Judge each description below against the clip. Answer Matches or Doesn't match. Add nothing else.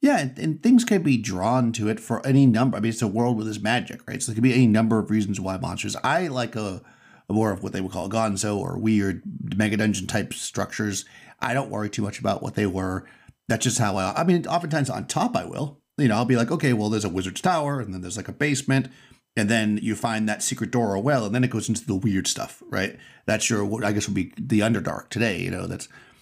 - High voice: Doesn't match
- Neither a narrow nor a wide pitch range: Matches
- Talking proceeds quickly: Matches